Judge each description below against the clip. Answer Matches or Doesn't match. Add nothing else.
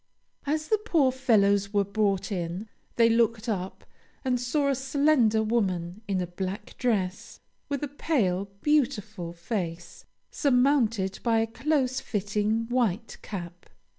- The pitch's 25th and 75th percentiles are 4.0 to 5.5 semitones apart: Matches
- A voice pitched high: Matches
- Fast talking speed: Doesn't match